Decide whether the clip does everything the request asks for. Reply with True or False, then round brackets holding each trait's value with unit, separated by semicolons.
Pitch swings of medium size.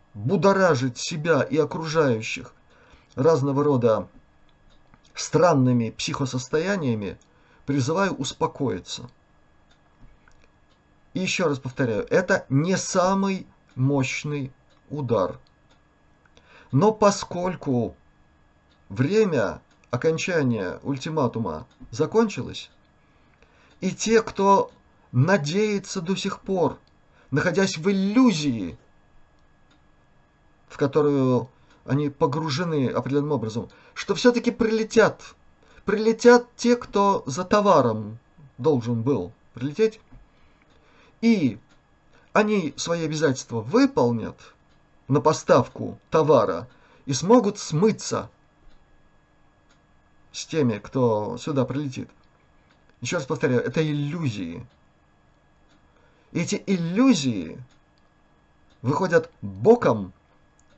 False (8.5 semitones)